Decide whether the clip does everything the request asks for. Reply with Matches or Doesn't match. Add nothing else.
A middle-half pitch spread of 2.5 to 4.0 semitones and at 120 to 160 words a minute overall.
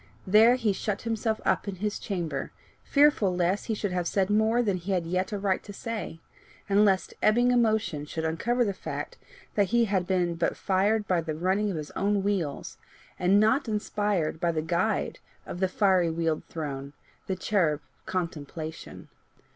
Doesn't match